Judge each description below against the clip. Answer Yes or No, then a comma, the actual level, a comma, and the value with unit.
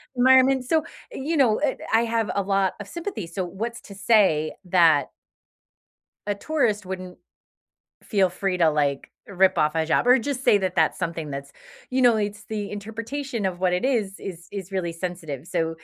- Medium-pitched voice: No, high, 195 Hz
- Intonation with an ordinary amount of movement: Yes, average, 4.8 semitones